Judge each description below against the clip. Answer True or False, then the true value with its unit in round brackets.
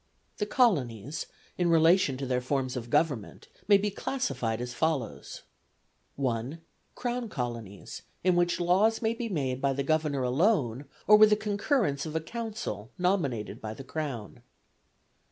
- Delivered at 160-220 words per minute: False (150 wpm)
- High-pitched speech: False (150 Hz)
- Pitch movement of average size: False (8.2 semitones)